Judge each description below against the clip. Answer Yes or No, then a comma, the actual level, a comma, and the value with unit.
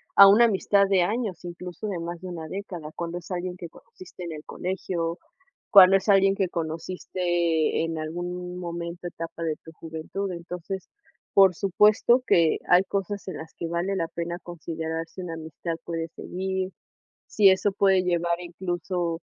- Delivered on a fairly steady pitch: Yes, narrow, 2.2 semitones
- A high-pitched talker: No, medium, 175 Hz